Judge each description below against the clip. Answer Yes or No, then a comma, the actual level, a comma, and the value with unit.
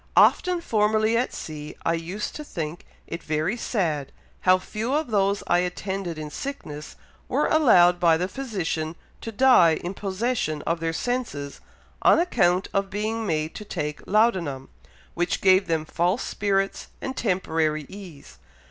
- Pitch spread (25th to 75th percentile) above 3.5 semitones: Yes, average, 5.0 semitones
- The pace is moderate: Yes, average, 150 wpm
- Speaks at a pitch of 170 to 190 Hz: Yes, medium, 185 Hz